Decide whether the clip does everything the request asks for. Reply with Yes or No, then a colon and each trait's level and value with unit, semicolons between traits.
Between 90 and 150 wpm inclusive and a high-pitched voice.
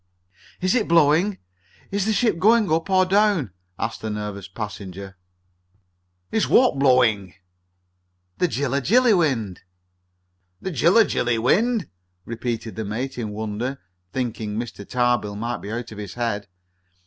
No: slow, 135 wpm; low, 125 Hz